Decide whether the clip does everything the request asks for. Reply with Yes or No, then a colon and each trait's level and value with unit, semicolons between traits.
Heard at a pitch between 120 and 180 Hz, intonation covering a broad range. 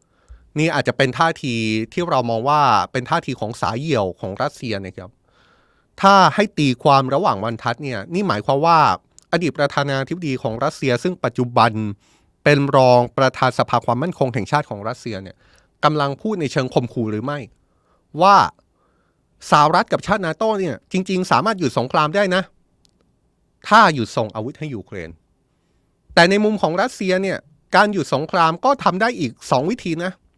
Yes: medium, 140 Hz; wide, 6.4 semitones